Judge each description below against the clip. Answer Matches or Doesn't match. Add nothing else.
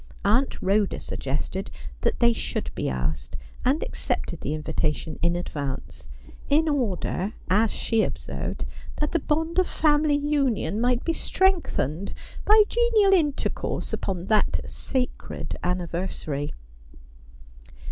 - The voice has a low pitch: Doesn't match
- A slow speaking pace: Matches